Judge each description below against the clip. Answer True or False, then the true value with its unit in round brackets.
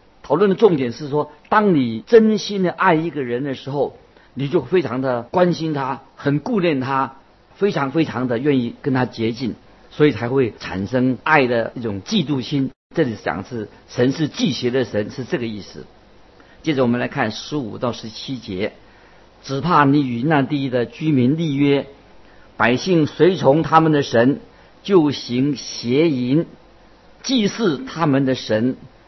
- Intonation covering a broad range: False (4.5 semitones)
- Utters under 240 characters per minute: True (230 characters per minute)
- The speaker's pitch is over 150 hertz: False (135 Hz)